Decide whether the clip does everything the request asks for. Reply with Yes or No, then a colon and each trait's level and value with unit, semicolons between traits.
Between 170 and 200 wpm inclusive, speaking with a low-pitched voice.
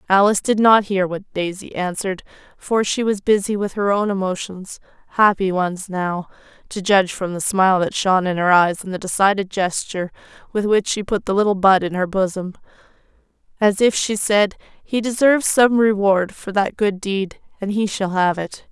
No: average, 185 wpm; high, 195 Hz